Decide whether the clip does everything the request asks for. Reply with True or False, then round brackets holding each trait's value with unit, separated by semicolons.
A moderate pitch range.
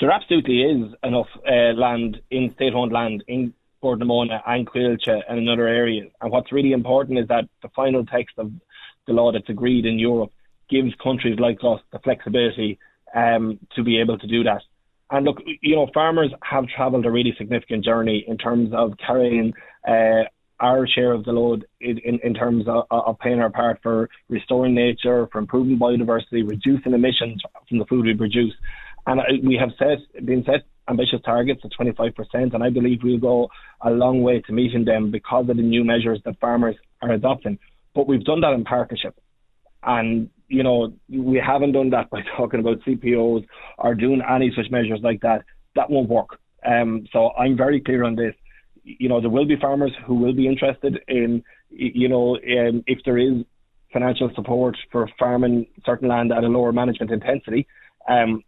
False (1.6 semitones)